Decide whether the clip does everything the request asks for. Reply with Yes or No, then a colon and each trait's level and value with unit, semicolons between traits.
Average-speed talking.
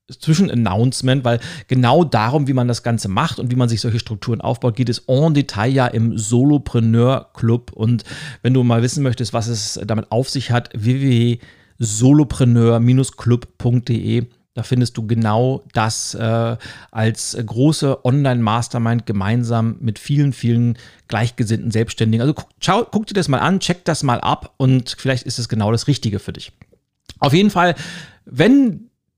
Yes: average, 155 wpm